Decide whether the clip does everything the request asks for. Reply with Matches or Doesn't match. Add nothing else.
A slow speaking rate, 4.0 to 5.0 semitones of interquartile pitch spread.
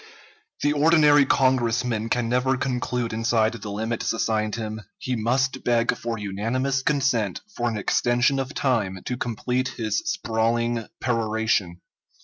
Doesn't match